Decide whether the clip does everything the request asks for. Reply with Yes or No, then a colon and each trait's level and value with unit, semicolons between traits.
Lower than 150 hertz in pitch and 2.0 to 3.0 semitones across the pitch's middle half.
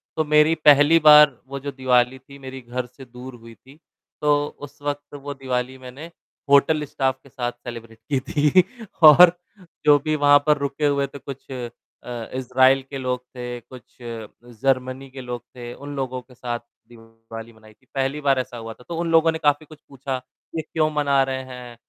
Yes: low, 135 Hz; average, 2.7 semitones